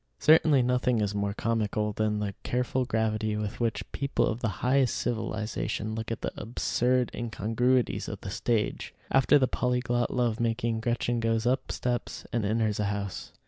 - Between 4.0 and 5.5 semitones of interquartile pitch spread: No, narrow, 2.5 semitones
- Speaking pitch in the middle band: No, low, 115 Hz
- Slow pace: No, average, 165 wpm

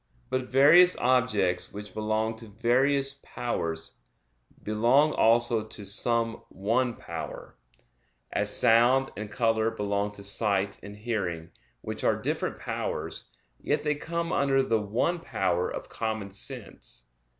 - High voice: No, low, 115 Hz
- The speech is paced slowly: Yes, slow, 130 wpm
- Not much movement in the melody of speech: No, average, 4.1 semitones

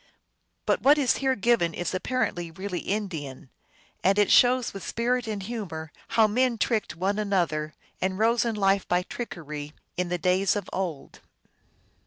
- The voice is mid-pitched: No, high, 195 Hz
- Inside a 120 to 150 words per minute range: No, average, 160 wpm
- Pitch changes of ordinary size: Yes, average, 4.7 semitones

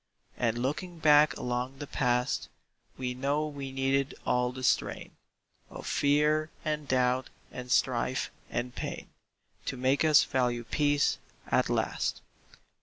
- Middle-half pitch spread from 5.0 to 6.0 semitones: No, average, 2.8 semitones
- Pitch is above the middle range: No, low, 135 Hz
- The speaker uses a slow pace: Yes, slow, 130 wpm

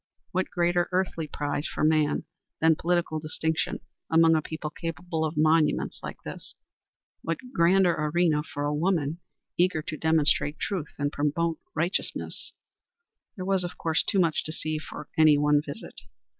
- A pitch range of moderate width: No, narrow, 2.2 semitones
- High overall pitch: No, medium, 160 Hz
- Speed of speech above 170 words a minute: No, average, 155 wpm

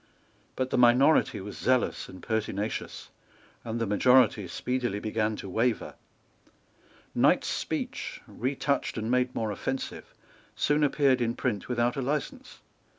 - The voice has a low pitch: Yes, low, 120 Hz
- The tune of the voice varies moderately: Yes, average, 3.0 semitones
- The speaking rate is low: Yes, slow, 130 wpm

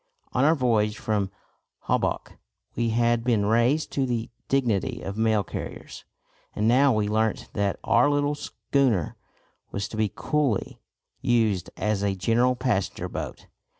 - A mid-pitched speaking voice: No, low, 115 Hz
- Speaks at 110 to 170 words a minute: Yes, average, 145 wpm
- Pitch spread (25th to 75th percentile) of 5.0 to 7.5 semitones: No, average, 3.3 semitones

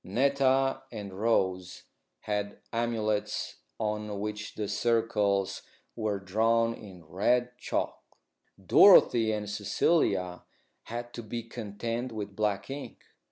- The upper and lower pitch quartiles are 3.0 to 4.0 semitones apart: No, narrow, 2.6 semitones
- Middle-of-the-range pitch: No, low, 105 Hz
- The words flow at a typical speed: No, slow, 110 wpm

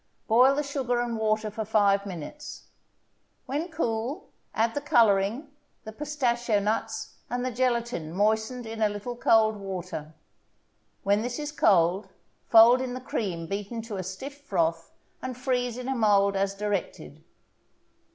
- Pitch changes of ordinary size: Yes, average, 3.9 semitones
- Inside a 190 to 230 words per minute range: No, average, 150 wpm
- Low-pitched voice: No, high, 225 Hz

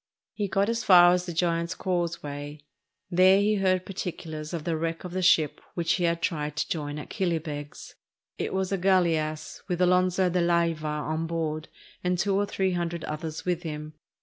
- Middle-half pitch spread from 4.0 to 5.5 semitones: No, average, 2.8 semitones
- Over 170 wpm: Yes, average, 185 wpm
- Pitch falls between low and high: Yes, medium, 170 Hz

